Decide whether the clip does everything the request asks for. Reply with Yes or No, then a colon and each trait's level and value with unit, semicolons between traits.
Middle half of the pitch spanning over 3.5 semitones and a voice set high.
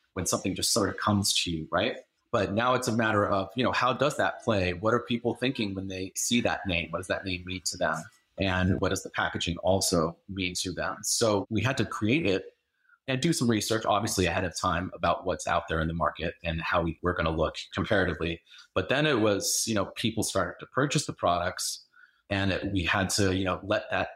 No: average, 4.1 semitones; very low, 95 Hz